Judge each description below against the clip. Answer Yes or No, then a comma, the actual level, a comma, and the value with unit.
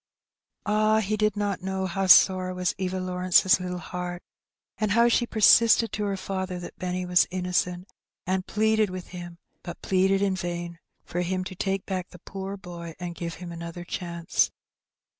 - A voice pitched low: No, medium, 185 Hz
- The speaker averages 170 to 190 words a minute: Yes, average, 175 wpm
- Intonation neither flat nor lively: No, narrow, 1.7 semitones